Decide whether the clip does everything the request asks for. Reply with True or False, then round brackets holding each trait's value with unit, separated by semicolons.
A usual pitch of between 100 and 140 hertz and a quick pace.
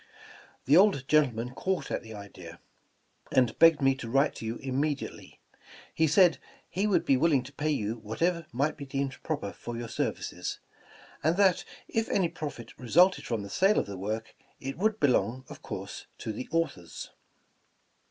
False (135 Hz; 180 wpm)